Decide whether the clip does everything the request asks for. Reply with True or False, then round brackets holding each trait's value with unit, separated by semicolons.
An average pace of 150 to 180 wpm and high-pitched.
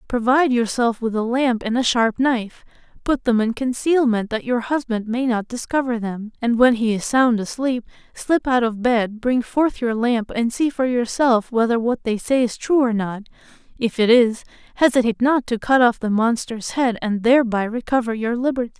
False (200 wpm; 240 Hz)